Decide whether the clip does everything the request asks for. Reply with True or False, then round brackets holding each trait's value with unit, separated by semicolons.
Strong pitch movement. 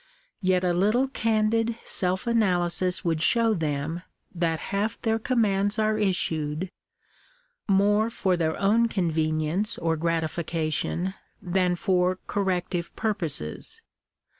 False (4.3 semitones)